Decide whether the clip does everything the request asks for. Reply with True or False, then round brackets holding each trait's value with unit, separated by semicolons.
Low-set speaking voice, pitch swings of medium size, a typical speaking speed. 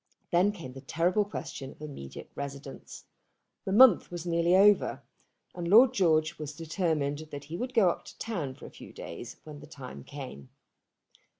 False (165 Hz; 4.9 semitones; 180 wpm)